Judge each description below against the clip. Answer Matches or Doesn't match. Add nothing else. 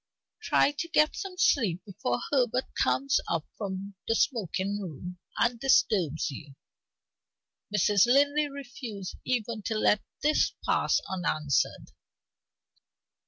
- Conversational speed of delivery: Doesn't match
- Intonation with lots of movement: Matches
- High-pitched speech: Matches